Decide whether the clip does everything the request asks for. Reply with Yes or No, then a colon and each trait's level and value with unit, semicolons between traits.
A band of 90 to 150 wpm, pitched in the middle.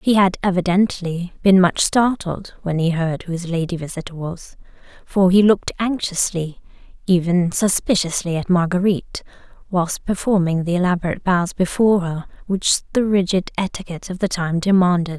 Yes: average, 140 wpm; medium, 180 Hz